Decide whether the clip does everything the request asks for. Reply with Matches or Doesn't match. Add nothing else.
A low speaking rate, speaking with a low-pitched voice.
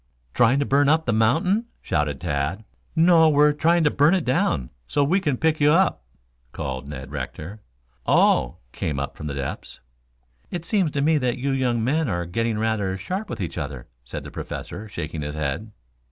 Doesn't match